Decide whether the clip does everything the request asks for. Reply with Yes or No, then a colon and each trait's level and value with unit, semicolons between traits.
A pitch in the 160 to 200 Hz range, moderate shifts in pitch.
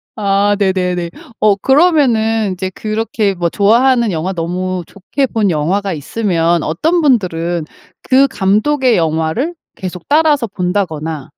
Yes: high, 195 Hz; average, 5.0 semitones